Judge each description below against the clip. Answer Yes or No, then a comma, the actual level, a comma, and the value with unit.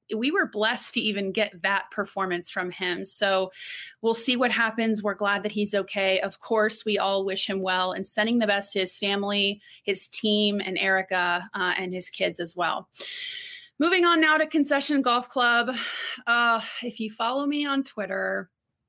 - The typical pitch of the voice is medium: No, high, 210 Hz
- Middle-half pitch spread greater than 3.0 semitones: Yes, average, 3.9 semitones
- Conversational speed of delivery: Yes, average, 185 wpm